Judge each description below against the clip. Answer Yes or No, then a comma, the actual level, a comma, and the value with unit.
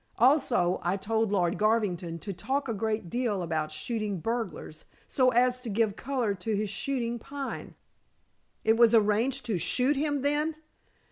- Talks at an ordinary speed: Yes, average, 155 wpm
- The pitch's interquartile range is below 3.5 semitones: No, average, 4.1 semitones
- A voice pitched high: Yes, high, 225 Hz